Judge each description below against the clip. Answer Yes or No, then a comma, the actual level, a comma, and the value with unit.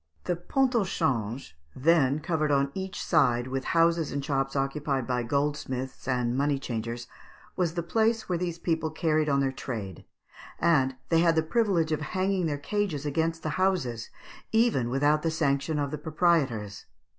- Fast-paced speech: No, average, 170 wpm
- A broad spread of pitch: No, average, 4.1 semitones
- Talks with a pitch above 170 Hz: No, medium, 150 Hz